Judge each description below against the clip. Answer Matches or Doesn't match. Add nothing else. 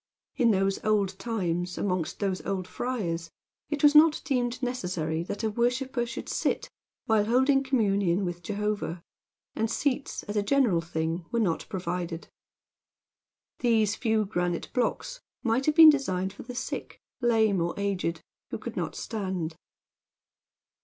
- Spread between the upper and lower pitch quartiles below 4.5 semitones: Doesn't match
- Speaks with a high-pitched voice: Matches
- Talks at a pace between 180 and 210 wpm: Doesn't match